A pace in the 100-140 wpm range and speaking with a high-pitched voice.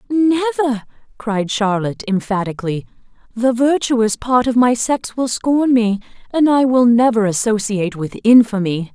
Yes: slow, 135 wpm; high, 230 Hz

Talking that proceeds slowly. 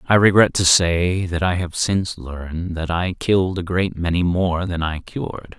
No: fast, 205 wpm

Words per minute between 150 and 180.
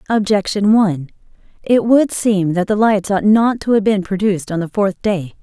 No: average, 200 wpm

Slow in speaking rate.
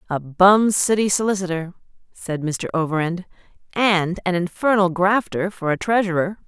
Yes: slow, 120 wpm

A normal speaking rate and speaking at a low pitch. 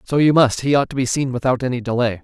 No: fast, 295 wpm; low, 130 Hz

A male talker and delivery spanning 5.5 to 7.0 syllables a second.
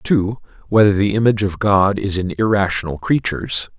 Yes: male; 5.9 syllables/s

